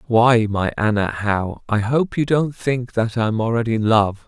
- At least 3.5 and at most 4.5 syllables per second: No, 5.1 syllables/s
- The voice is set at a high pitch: No, low, 115 Hz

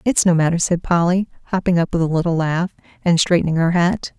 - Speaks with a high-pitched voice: No, medium, 175 Hz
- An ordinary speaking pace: No, fast, 215 wpm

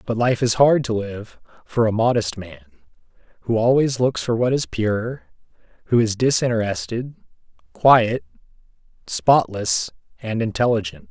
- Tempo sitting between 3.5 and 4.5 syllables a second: Yes, 4.4 syllables/s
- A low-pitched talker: Yes, low, 115 Hz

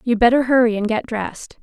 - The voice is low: No, high, 235 Hz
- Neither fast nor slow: No, fast, 220 wpm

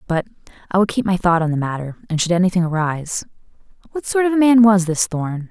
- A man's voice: No, female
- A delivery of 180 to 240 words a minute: Yes, fast, 205 wpm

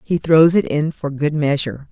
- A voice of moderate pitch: Yes, medium, 150 Hz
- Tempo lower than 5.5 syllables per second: Yes, 5.0 syllables/s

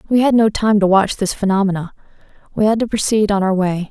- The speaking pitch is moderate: No, high, 205 Hz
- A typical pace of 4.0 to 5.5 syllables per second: No, 6.4 syllables/s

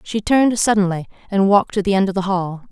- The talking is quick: Yes, fast, 245 wpm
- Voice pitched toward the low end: No, high, 195 Hz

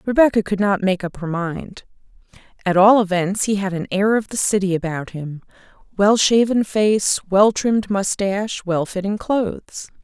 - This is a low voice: No, high, 200 Hz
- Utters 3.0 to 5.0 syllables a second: Yes, 4.7 syllables/s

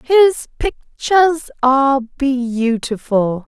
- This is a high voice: Yes, very high, 270 Hz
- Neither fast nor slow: No, slow, 65 wpm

